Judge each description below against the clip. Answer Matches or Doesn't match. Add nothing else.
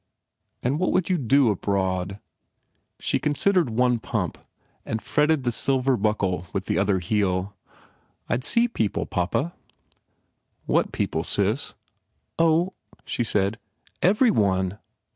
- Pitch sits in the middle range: Doesn't match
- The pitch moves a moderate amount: Doesn't match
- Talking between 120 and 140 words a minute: Matches